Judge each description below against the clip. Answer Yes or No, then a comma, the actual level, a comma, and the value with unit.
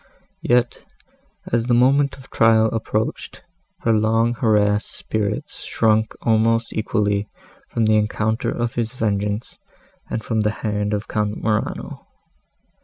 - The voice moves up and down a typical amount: No, narrow, 1.5 semitones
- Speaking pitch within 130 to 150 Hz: No, low, 110 Hz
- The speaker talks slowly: Yes, slow, 125 wpm